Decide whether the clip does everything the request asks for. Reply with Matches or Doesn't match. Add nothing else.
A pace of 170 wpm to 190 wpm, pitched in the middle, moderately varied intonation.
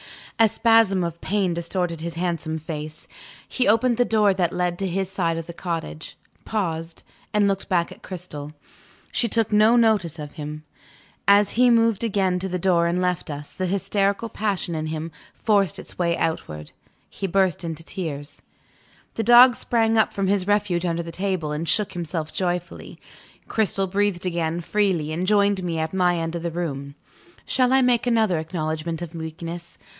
Matches